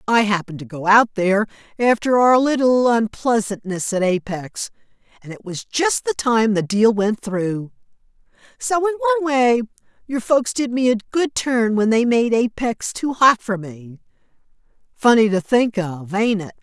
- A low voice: No, high, 225 Hz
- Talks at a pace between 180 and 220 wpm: No, average, 170 wpm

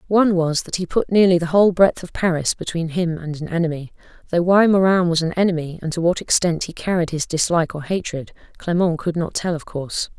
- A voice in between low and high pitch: Yes, medium, 170 Hz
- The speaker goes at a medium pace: No, fast, 225 wpm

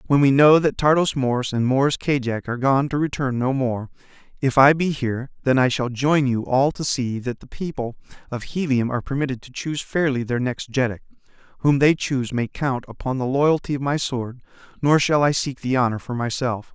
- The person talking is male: Yes, male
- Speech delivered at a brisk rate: Yes, fast, 210 wpm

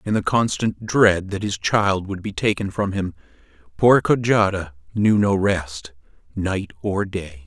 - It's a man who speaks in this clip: Yes, male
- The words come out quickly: No, average, 160 wpm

